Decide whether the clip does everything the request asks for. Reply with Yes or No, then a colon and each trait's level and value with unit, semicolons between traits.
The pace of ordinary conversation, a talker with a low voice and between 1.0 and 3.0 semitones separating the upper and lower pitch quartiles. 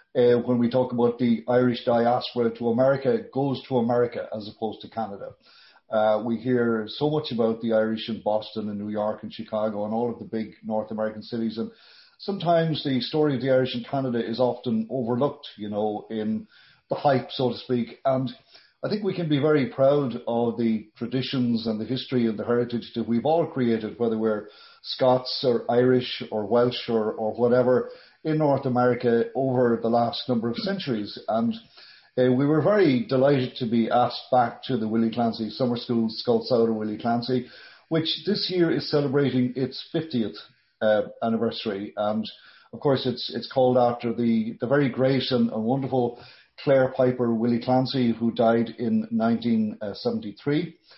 Yes: average, 175 wpm; low, 120 Hz; average, 2.7 semitones